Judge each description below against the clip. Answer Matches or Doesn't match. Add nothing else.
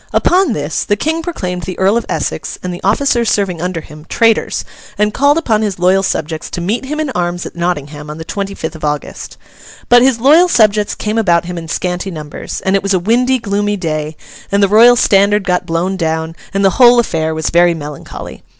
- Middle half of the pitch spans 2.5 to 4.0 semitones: Doesn't match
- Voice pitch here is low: Doesn't match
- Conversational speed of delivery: Doesn't match